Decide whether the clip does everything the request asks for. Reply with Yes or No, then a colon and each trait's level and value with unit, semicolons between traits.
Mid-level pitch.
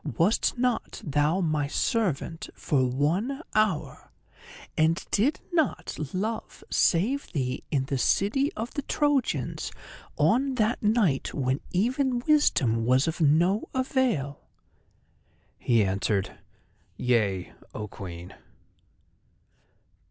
Yes: medium, 170 Hz